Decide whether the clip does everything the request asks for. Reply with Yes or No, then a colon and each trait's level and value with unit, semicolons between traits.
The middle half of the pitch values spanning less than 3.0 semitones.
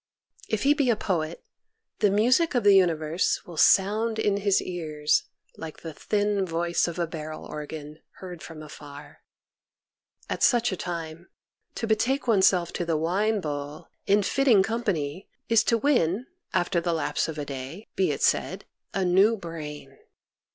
No: average, 5.0 semitones